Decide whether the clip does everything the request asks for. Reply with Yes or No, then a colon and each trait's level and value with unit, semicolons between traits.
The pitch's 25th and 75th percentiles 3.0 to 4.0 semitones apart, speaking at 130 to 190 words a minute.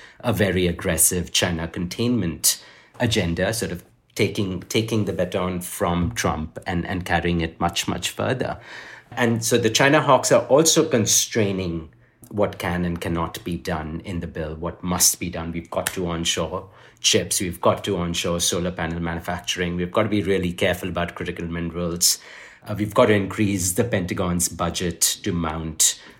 Yes: average, 3.4 semitones; average, 165 wpm